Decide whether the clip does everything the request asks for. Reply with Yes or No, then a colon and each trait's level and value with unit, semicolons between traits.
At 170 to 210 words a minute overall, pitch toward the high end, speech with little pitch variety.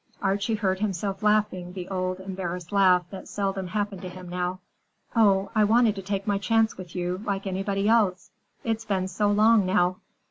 Yes: average, 180 wpm; high, 195 Hz; narrow, 2.2 semitones